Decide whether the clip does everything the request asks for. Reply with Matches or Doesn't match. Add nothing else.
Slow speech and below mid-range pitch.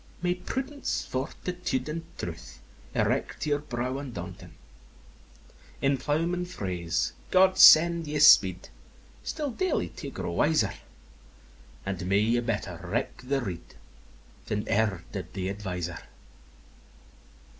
Matches